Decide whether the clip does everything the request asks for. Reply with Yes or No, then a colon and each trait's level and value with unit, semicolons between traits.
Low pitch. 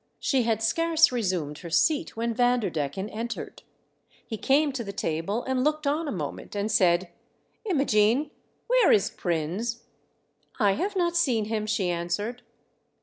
No: high, 225 Hz